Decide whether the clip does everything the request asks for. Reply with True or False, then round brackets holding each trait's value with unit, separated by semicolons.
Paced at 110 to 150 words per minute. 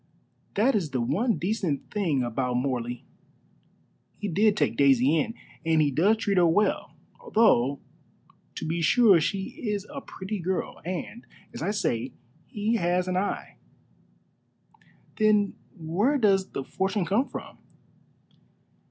True (135 wpm)